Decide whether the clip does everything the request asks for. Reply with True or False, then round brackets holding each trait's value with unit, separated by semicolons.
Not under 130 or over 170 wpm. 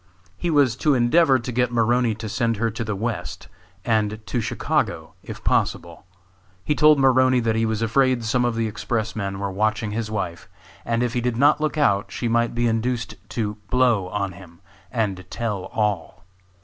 False (190 wpm)